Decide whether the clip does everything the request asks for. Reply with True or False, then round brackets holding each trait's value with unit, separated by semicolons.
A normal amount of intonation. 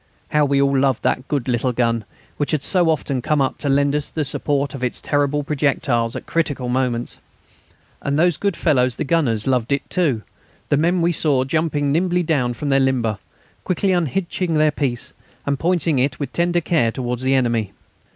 True (3.8 semitones)